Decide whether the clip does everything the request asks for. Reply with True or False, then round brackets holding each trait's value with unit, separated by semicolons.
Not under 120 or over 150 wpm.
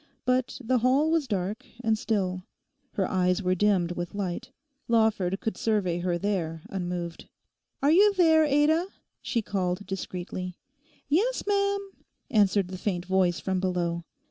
True (145 wpm)